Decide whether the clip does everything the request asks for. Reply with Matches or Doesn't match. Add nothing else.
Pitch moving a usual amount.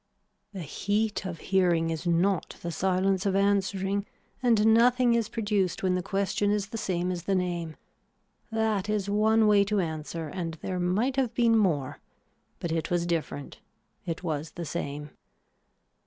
Matches